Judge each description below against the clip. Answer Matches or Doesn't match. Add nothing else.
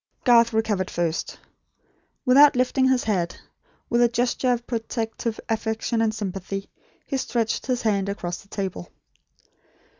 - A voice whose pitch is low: Doesn't match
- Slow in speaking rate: Matches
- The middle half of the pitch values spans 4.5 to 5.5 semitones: Doesn't match